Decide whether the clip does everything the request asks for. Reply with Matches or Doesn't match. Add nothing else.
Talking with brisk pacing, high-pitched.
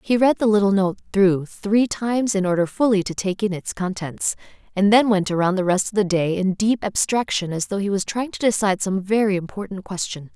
Matches